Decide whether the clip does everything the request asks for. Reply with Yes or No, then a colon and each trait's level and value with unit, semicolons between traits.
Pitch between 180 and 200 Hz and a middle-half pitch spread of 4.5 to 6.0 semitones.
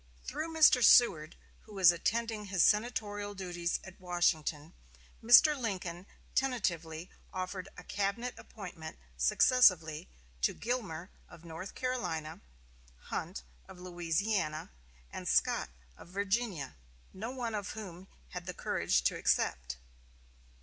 Yes: high, 190 Hz; average, 5.1 semitones